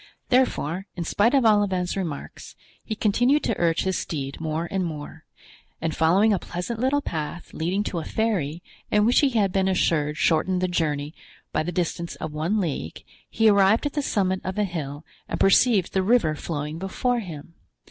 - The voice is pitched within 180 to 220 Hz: Yes, medium, 185 Hz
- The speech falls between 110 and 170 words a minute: No, average, 185 wpm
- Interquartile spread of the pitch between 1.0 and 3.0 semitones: No, average, 4.7 semitones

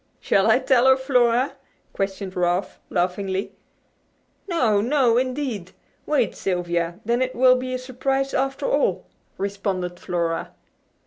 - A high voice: Yes, high, 235 Hz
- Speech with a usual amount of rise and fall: No, wide, 5.7 semitones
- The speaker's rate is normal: No, slow, 125 wpm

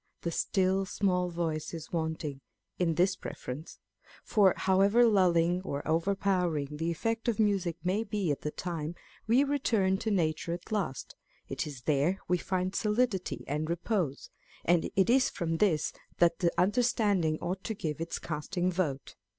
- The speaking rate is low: No, average, 165 wpm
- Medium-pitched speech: Yes, medium, 180 Hz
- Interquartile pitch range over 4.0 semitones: No, average, 3.7 semitones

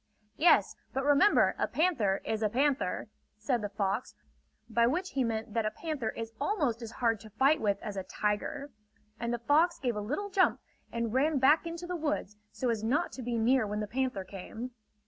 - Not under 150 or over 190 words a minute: No, fast, 205 wpm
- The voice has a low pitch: No, high, 240 Hz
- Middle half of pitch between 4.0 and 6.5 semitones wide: Yes, average, 5.1 semitones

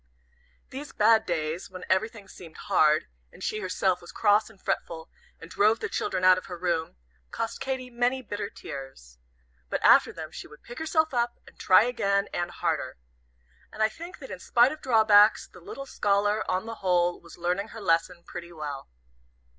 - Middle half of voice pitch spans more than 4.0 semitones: Yes, average, 4.6 semitones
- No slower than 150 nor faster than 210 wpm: Yes, average, 185 wpm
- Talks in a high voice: Yes, high, 200 Hz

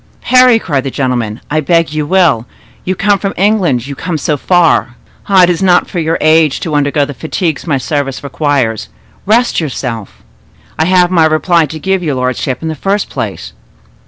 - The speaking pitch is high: No, medium, 160 Hz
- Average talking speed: Yes, average, 185 wpm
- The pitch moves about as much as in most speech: Yes, average, 4.5 semitones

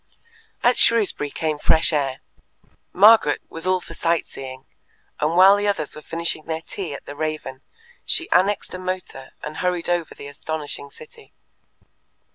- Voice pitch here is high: No, medium, 165 Hz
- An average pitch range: Yes, average, 3.8 semitones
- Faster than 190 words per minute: No, average, 155 wpm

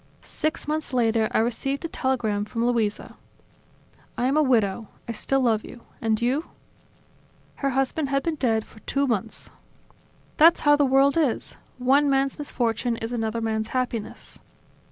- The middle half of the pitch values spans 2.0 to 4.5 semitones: Yes, average, 3.5 semitones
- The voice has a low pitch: No, very high, 250 Hz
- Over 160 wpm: No, average, 155 wpm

